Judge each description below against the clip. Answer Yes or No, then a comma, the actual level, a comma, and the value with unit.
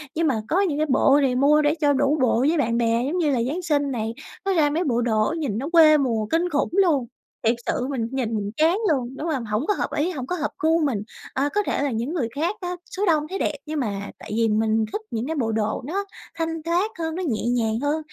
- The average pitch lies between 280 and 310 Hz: Yes, very high, 285 Hz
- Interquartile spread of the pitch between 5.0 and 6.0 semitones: Yes, wide, 5.5 semitones